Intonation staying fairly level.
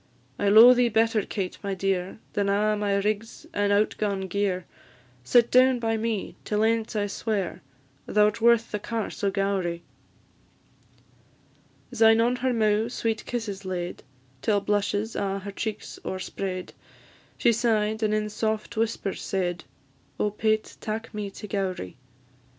Yes: narrow, 2.2 semitones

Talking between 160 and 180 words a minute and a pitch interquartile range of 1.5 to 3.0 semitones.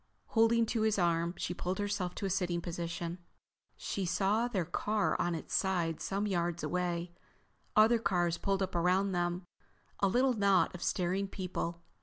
Yes: average, 165 wpm; narrow, 2.6 semitones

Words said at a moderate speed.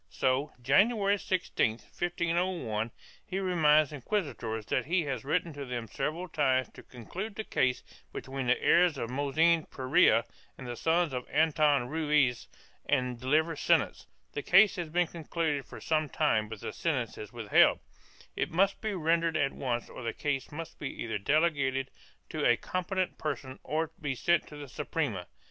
Yes: average, 165 wpm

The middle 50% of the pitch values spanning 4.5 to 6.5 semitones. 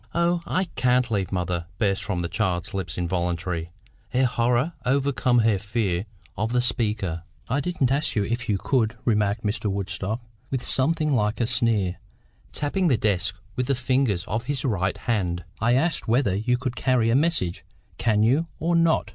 Yes: average, 4.8 semitones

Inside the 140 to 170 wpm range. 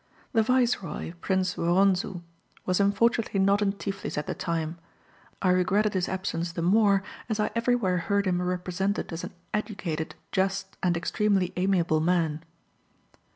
Yes: average, 145 wpm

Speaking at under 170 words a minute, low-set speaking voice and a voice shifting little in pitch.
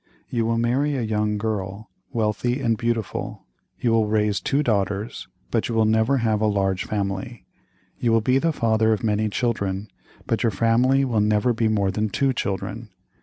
No: average, 180 wpm; low, 110 Hz; narrow, 2.0 semitones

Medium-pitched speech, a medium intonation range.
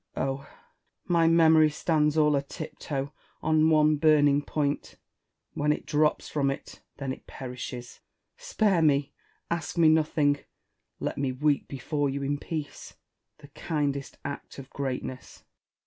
No: medium, 145 Hz; narrow, 2.1 semitones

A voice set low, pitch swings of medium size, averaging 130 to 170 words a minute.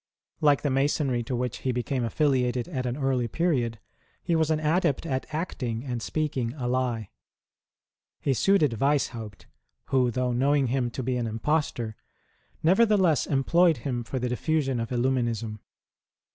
Yes: low, 130 Hz; average, 3.7 semitones; average, 150 wpm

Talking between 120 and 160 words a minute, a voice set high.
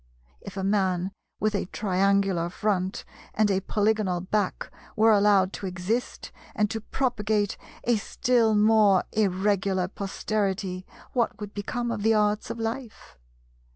Yes: slow, 135 wpm; high, 205 Hz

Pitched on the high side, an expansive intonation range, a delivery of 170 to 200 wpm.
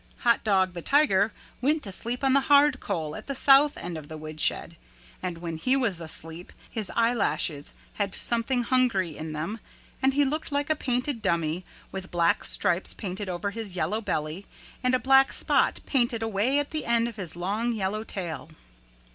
Yes: high, 215 Hz; wide, 6.7 semitones; average, 185 wpm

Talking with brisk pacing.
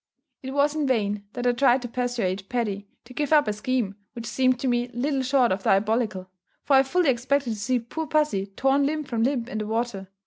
Yes: fast, 220 wpm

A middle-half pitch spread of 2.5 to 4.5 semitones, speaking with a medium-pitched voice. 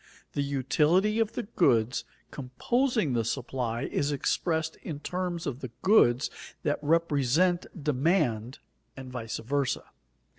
No: wide, 5.5 semitones; medium, 145 Hz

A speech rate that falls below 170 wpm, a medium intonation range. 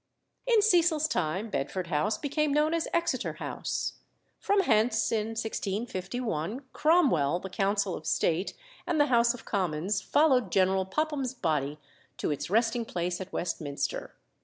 No: average, 140 wpm; wide, 8.2 semitones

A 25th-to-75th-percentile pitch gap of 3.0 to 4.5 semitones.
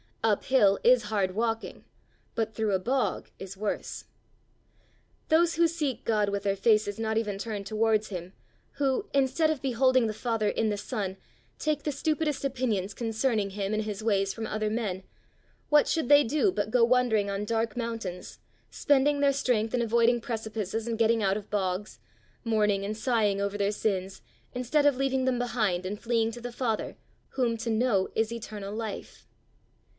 Yes: average, 3.5 semitones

